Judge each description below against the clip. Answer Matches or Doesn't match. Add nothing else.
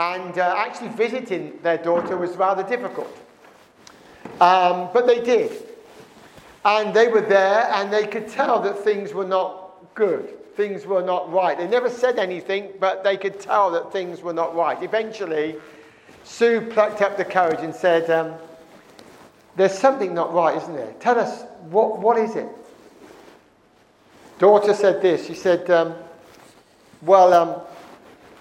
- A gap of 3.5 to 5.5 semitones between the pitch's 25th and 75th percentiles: Matches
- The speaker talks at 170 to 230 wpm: Doesn't match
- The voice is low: Doesn't match